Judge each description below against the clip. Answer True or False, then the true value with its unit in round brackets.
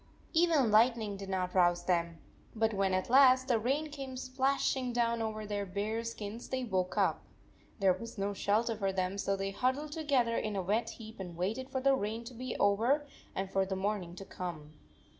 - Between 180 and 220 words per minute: True (200 wpm)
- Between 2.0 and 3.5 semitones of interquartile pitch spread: False (4.8 semitones)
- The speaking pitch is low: False (215 Hz)